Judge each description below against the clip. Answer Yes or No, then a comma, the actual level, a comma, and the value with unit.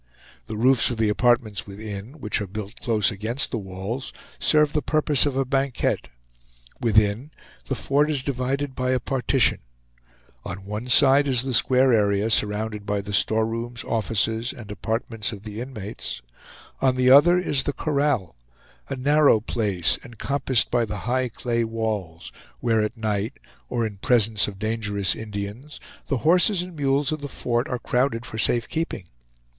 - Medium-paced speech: Yes, average, 160 wpm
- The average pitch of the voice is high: No, low, 115 Hz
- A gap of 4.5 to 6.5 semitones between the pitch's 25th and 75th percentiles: No, average, 4.1 semitones